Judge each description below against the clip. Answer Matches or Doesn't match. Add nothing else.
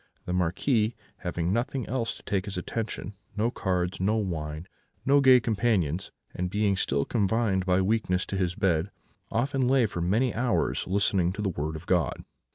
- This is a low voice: Matches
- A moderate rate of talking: Matches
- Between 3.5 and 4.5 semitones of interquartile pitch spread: Matches